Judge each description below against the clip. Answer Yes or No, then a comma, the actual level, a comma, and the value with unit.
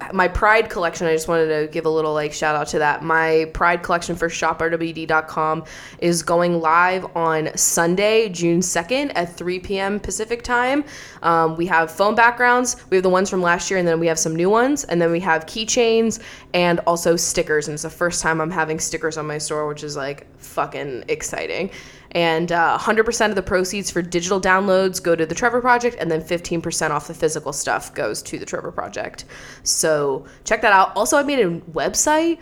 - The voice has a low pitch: No, medium, 170 Hz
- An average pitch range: Yes, average, 3.9 semitones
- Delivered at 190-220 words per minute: Yes, fast, 205 wpm